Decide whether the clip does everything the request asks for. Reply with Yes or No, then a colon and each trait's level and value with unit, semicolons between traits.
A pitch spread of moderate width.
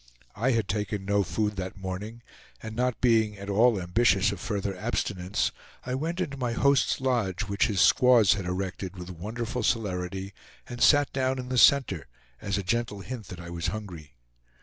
Yes: average, 4.2 semitones